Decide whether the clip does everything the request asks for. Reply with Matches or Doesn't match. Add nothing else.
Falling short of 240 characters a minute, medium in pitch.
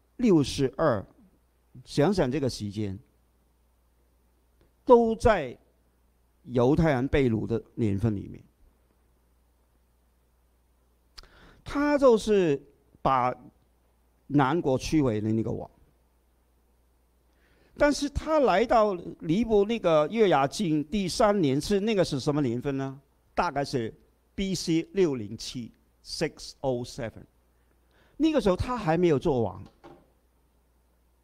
Doesn't match